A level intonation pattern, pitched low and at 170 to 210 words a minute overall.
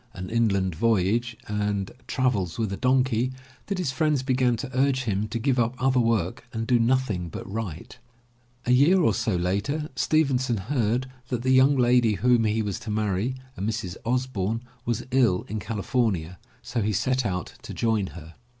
No: average, 4.1 semitones; low, 115 Hz; average, 175 wpm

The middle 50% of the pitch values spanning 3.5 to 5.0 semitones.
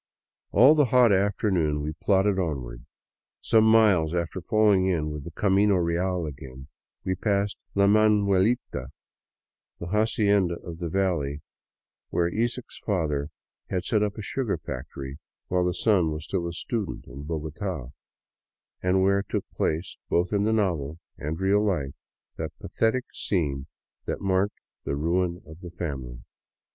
Yes: average, 4.7 semitones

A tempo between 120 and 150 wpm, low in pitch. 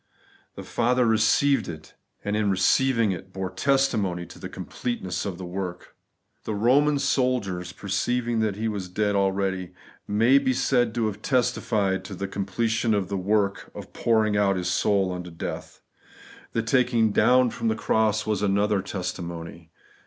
No: average, 160 wpm; low, 105 Hz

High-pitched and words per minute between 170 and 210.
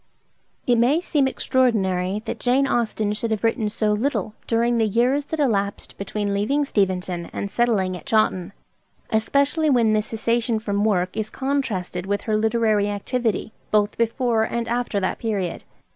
No: high, 220 Hz; average, 160 wpm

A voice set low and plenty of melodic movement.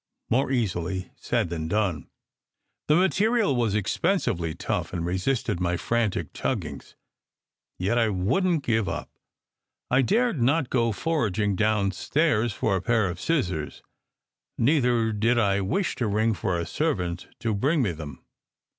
Yes: low, 110 Hz; wide, 6.2 semitones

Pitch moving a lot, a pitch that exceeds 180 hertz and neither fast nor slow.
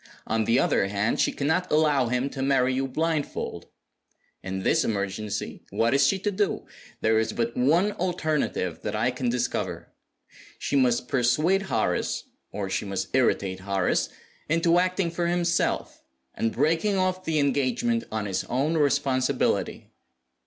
No: wide, 6.5 semitones; low, 130 Hz; average, 150 wpm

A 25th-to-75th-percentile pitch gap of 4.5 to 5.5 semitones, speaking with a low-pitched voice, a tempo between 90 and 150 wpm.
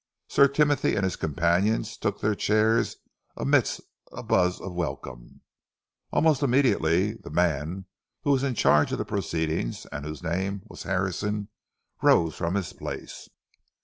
Yes: average, 4.8 semitones; very low, 95 Hz; average, 145 wpm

